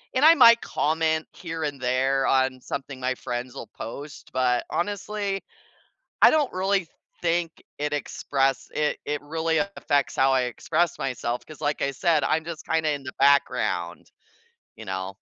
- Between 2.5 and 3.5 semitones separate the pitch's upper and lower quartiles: No, average, 4.1 semitones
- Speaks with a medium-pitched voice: Yes, medium, 145 Hz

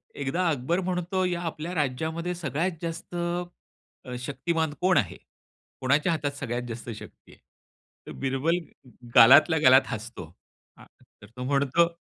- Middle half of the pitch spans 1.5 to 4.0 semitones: No, average, 4.7 semitones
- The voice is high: No, medium, 155 Hz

